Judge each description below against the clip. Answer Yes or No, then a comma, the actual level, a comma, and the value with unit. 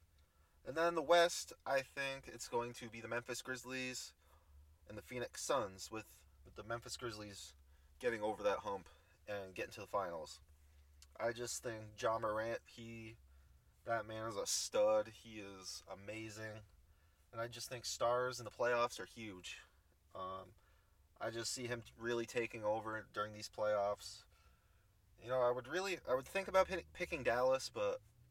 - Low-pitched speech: Yes, low, 110 Hz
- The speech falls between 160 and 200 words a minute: Yes, average, 165 wpm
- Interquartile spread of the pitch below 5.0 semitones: No, wide, 5.6 semitones